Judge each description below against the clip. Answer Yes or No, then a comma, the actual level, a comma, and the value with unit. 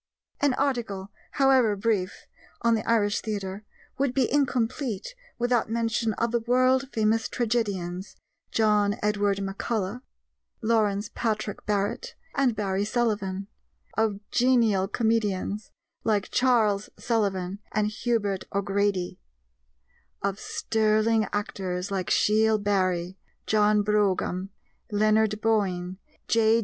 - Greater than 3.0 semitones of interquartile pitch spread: No, narrow, 2.5 semitones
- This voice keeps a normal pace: No, slow, 105 wpm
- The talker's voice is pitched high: Yes, high, 215 Hz